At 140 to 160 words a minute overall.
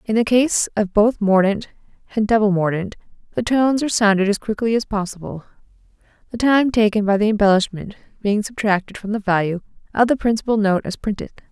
No: average, 175 wpm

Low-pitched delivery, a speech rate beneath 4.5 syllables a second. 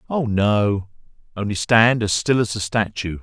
Yes: low, 105 Hz; 4.3 syllables/s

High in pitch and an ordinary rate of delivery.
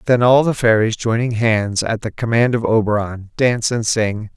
No: low, 115 Hz; average, 195 wpm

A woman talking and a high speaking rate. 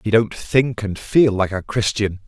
No: male; fast, 210 wpm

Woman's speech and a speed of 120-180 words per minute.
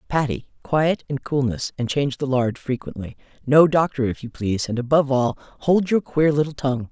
No: female; average, 190 wpm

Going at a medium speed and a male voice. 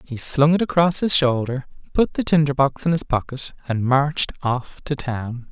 Yes: average, 195 wpm; male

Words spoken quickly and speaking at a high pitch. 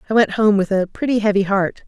Yes: fast, 255 wpm; high, 205 Hz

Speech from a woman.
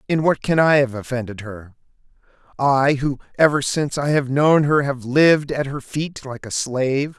No: male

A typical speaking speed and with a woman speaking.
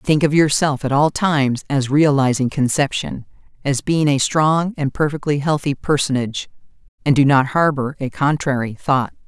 Yes: average, 155 wpm; female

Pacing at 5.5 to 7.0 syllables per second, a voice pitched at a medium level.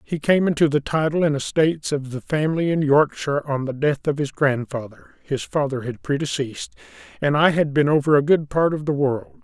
Yes: 5.6 syllables/s; medium, 145 Hz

